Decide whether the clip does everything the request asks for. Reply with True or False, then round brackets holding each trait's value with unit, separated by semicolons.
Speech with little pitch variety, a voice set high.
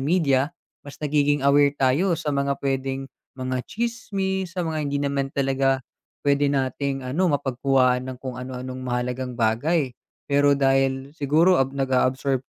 False (1.8 semitones; 135 Hz)